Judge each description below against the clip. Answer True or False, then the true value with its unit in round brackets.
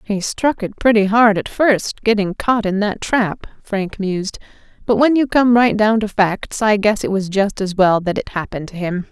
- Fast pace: True (225 wpm)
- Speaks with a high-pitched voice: True (205 Hz)